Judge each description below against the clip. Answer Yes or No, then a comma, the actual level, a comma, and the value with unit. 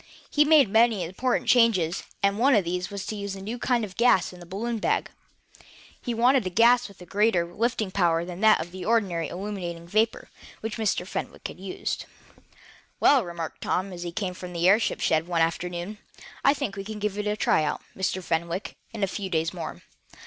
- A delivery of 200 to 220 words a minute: Yes, fast, 205 wpm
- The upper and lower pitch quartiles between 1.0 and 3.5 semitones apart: No, average, 4.1 semitones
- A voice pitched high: Yes, high, 195 Hz